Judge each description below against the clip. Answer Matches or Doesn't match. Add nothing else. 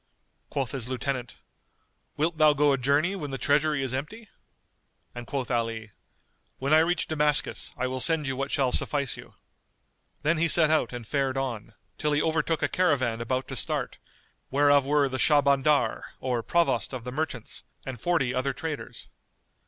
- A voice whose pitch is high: Doesn't match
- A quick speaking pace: Doesn't match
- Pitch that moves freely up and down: Doesn't match